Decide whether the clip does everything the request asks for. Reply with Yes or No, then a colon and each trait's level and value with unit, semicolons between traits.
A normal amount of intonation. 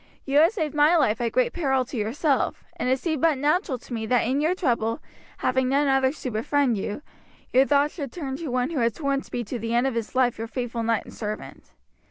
Yes: average, 3.7 semitones